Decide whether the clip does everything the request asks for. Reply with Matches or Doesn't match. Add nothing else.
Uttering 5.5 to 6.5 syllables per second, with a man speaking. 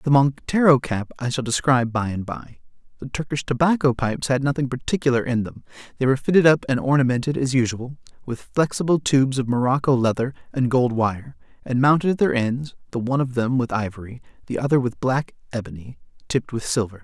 Matches